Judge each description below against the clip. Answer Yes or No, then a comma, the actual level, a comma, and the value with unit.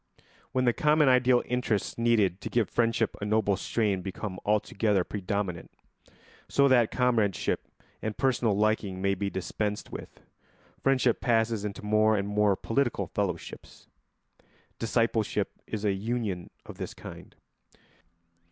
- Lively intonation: No, average, 3.0 semitones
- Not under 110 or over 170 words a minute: Yes, slow, 135 wpm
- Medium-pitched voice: No, low, 110 Hz